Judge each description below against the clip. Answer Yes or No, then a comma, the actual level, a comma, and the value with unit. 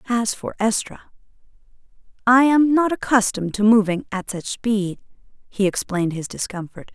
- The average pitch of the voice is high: Yes, high, 215 Hz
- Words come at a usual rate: No, slow, 130 wpm